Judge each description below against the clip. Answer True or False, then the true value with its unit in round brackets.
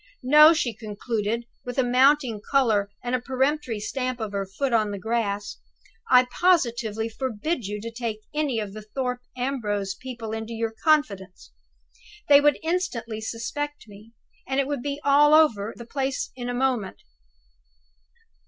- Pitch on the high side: True (240 Hz)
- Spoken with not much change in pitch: False (4.1 semitones)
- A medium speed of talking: True (155 wpm)